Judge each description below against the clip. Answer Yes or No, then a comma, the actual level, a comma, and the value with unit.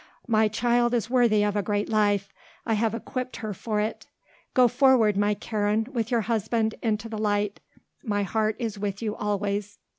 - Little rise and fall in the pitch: Yes, narrow, 1.9 semitones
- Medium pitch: No, high, 215 Hz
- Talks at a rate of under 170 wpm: No, average, 180 wpm